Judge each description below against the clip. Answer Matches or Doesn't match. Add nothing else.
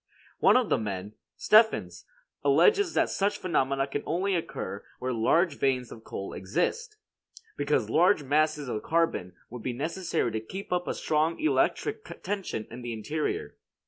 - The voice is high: Doesn't match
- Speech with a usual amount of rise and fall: Doesn't match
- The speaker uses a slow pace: Doesn't match